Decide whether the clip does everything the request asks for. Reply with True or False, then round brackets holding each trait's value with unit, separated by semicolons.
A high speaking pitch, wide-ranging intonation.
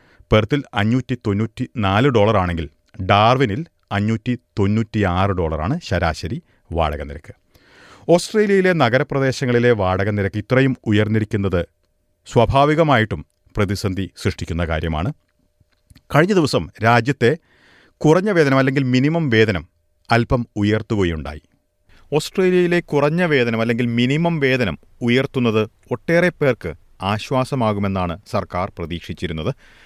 False (110 Hz; 6.1 semitones)